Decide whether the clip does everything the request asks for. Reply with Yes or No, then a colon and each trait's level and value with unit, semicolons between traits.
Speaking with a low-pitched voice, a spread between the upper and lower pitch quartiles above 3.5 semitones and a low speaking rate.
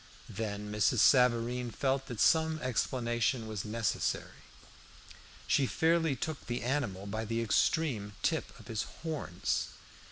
Yes: low, 120 Hz; average, 4.1 semitones; slow, 125 wpm